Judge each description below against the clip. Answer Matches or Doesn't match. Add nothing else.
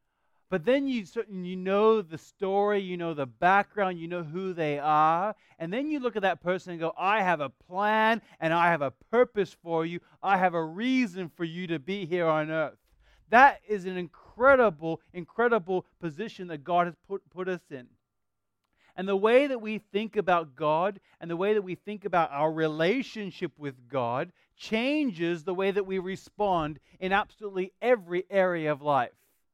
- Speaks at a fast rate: Doesn't match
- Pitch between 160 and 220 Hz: Matches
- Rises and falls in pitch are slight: Doesn't match